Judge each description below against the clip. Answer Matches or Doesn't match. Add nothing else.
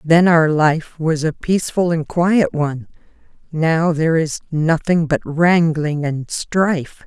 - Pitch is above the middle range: Doesn't match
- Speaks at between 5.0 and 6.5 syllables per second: Doesn't match